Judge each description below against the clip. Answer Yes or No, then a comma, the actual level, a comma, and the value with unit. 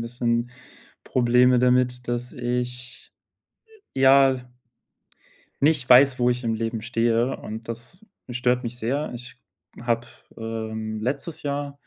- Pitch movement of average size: No, narrow, 1.6 semitones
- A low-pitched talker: Yes, low, 125 Hz